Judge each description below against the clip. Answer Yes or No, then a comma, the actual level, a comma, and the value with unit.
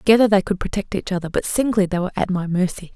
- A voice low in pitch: No, high, 190 Hz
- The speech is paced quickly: Yes, fast, 265 wpm